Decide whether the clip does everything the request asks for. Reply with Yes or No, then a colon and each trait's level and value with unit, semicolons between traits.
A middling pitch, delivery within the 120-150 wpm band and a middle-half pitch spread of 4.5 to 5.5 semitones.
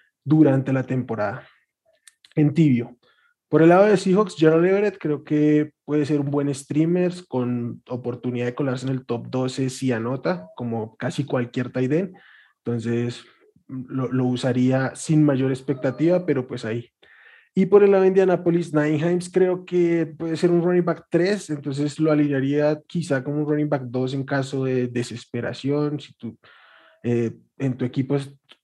No: medium, 145 Hz; average, 170 wpm; average, 4.8 semitones